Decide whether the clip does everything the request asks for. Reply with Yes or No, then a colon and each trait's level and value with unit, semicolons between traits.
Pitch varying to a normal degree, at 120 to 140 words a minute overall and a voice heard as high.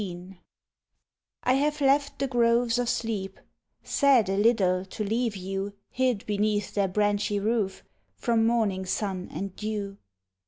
Yes: average, 3.4 semitones; slow, 135 wpm; high, 210 Hz